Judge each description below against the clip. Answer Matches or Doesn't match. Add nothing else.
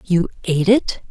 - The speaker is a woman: Matches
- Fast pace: Doesn't match